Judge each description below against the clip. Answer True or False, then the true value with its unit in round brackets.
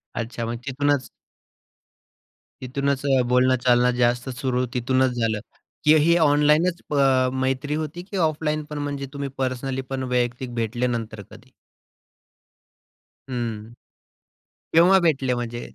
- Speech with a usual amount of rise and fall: True (3.1 semitones)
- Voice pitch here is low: True (130 Hz)